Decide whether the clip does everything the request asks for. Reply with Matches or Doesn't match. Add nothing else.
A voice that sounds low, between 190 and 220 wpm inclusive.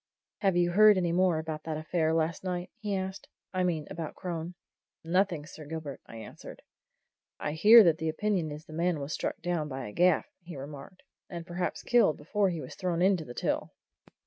Doesn't match